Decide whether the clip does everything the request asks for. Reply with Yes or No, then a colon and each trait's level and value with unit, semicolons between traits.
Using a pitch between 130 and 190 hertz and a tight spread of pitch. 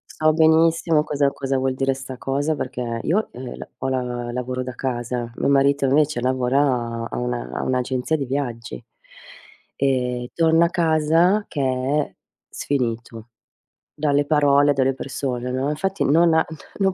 No: low, 135 Hz; average, 3.2 semitones